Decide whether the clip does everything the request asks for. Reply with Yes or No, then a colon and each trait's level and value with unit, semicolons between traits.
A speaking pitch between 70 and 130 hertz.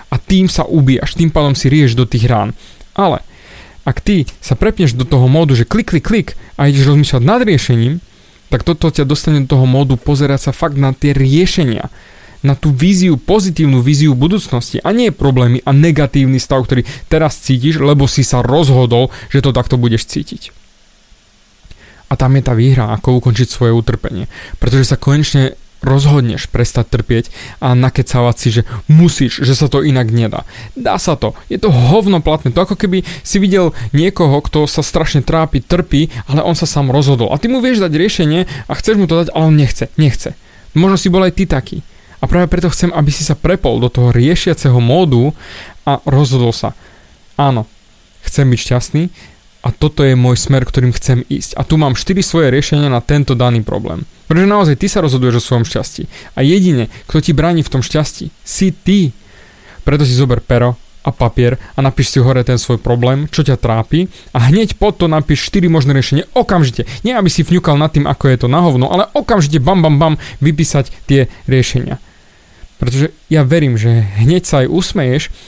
No: medium, 140 Hz